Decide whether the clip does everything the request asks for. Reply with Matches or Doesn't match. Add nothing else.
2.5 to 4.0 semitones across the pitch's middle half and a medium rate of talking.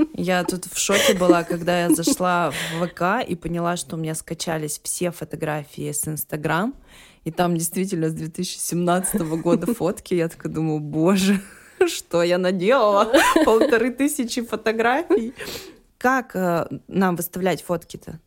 Matches